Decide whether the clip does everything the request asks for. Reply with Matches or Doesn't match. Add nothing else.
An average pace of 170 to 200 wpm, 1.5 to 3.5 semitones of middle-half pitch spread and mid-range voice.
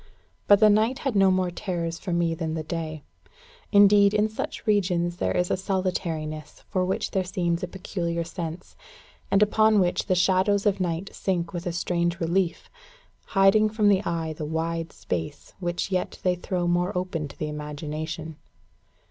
Matches